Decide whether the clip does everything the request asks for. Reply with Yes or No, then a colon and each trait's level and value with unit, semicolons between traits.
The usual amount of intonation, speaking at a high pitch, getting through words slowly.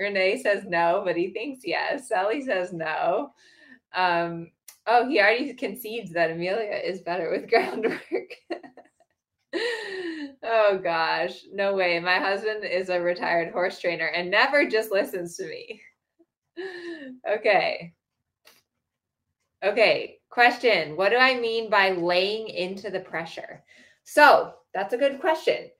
No: wide, 8.5 semitones; high, 205 Hz; slow, 130 wpm